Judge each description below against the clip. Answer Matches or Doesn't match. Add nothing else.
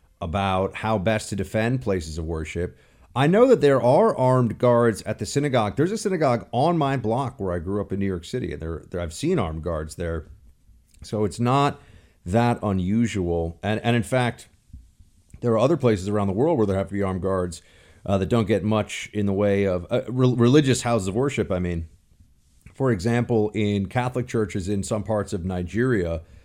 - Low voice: Matches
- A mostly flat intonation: Doesn't match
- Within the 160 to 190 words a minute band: Doesn't match